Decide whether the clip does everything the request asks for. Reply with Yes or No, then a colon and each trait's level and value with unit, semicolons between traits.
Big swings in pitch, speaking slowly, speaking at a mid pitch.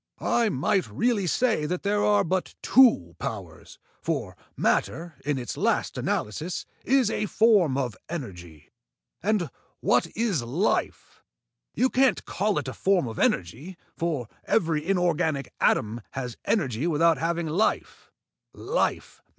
Yes: wide, 7.3 semitones; slow, 130 wpm; medium, 170 Hz